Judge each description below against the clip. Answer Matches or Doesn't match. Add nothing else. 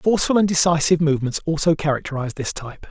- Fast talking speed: Doesn't match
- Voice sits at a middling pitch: Matches